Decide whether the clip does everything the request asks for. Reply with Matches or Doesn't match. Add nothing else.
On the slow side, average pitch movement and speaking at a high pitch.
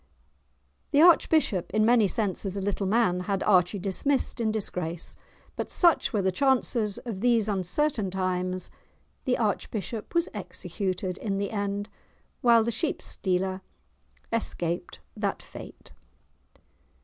Matches